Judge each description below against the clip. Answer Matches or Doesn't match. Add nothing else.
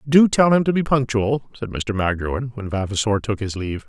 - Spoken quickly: Matches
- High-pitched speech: Doesn't match